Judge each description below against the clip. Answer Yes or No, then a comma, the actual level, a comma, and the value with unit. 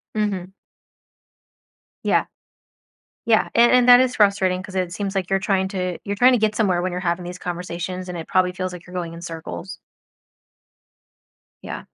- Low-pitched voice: No, medium, 185 Hz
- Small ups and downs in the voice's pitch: Yes, narrow, 2.3 semitones